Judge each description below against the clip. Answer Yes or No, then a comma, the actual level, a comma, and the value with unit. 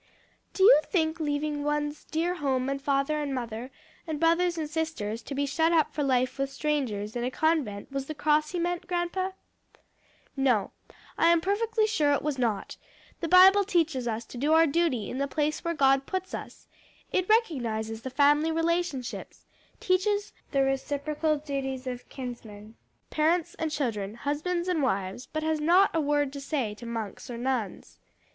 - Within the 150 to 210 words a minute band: Yes, average, 175 wpm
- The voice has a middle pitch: No, very high, 295 Hz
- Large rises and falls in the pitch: No, average, 4.2 semitones